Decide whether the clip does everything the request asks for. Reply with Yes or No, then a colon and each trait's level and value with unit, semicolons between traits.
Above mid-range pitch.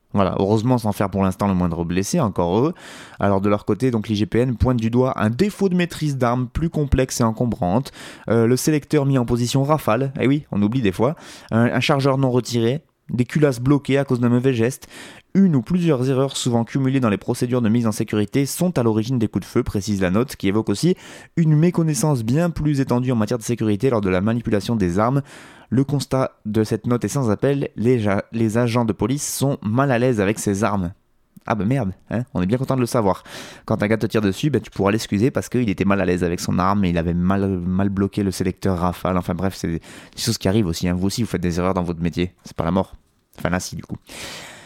No: low, 115 Hz